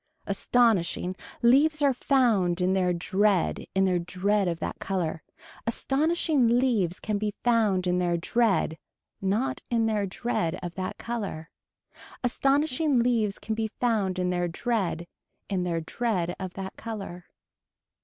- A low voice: No, high, 200 Hz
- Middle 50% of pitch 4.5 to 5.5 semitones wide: Yes, average, 4.9 semitones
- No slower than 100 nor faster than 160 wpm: Yes, average, 140 wpm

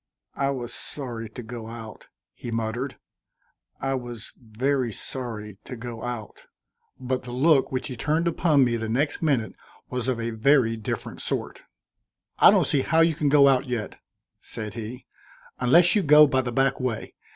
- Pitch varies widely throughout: No, average, 3.3 semitones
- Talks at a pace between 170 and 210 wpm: Yes, average, 175 wpm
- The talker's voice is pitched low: Yes, low, 125 Hz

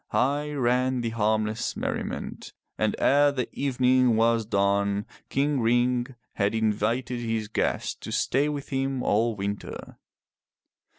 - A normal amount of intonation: Yes, average, 3.3 semitones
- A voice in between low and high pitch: No, low, 120 Hz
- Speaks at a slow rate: Yes, slow, 125 wpm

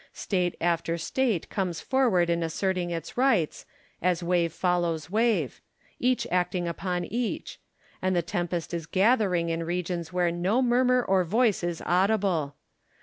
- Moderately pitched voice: Yes, medium, 180 Hz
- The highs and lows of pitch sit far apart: No, average, 3.3 semitones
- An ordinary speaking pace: Yes, average, 145 wpm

